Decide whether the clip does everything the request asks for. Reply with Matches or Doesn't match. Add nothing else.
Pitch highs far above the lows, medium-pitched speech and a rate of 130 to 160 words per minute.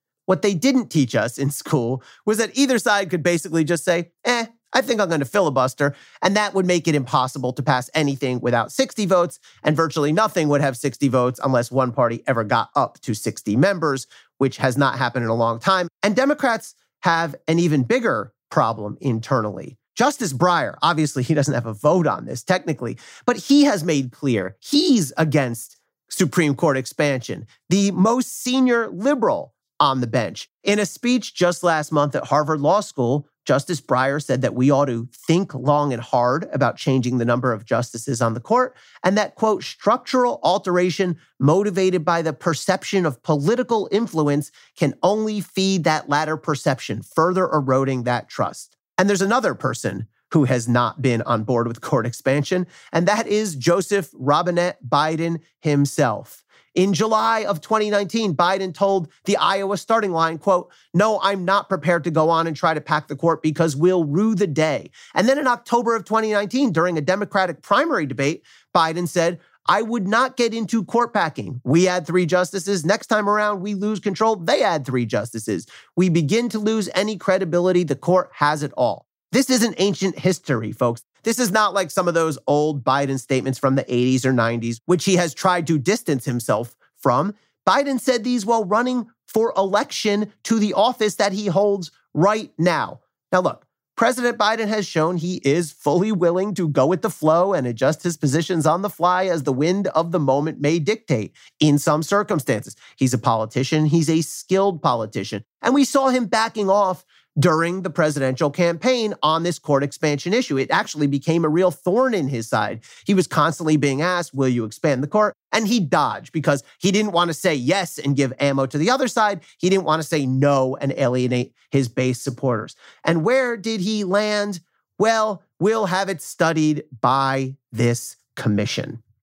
Doesn't match